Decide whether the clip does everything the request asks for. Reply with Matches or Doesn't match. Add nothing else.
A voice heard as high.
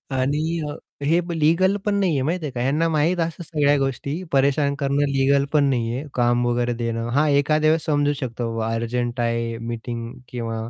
Doesn't match